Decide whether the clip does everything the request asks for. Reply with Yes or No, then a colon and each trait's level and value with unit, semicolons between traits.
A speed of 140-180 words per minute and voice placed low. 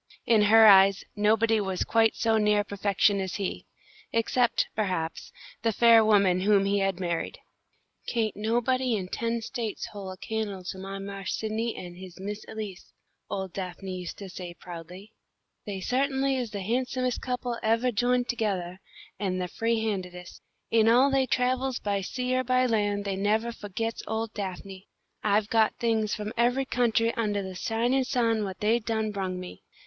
No: average, 170 wpm; high, 215 Hz